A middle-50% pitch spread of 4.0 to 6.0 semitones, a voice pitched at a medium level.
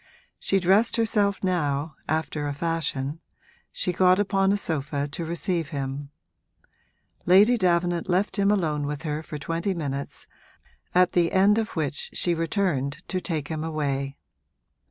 Yes: average, 4.3 semitones; medium, 165 Hz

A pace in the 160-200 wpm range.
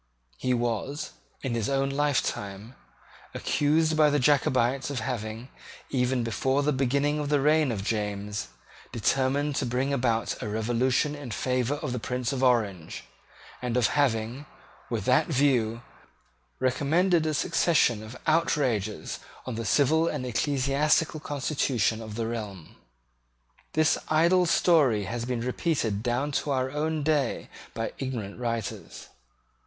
No: average, 140 wpm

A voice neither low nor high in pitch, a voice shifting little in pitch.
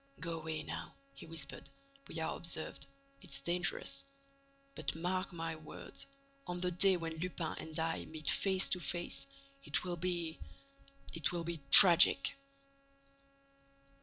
Yes: medium, 170 Hz; narrow, 2.1 semitones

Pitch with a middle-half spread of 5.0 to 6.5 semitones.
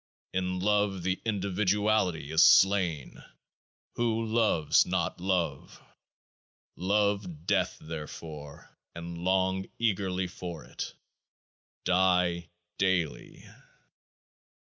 No: average, 2.8 semitones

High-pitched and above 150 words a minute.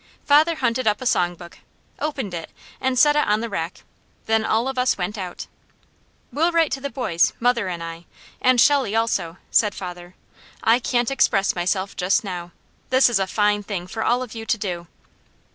Yes: high, 220 Hz; average, 195 wpm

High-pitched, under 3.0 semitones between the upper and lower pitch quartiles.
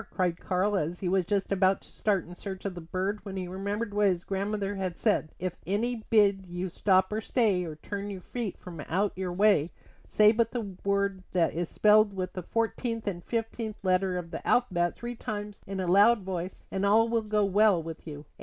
Yes: high, 195 Hz; narrow, 2.5 semitones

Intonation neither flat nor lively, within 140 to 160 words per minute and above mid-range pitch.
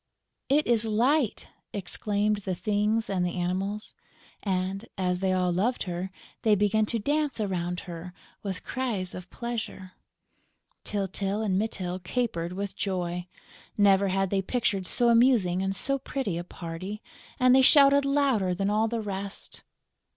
Yes: average, 3.8 semitones; average, 150 wpm; high, 200 Hz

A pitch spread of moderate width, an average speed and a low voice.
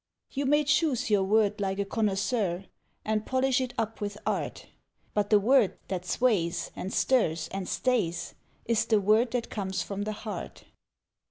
No: average, 4.2 semitones; average, 165 wpm; high, 210 Hz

